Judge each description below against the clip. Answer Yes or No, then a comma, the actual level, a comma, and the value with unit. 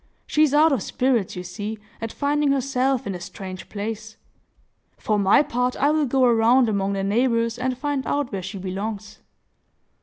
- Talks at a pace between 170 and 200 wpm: Yes, average, 180 wpm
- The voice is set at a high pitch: Yes, high, 230 Hz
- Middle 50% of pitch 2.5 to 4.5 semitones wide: No, average, 5.0 semitones